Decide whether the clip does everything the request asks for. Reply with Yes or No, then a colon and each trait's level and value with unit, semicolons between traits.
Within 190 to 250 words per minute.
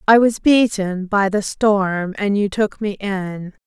No: average, 180 wpm